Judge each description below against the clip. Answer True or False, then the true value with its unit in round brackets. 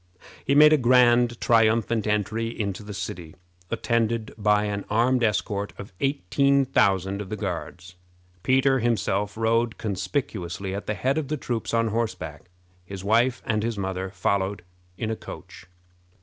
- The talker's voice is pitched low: True (110 Hz)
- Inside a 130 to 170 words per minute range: True (150 wpm)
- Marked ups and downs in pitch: False (3.3 semitones)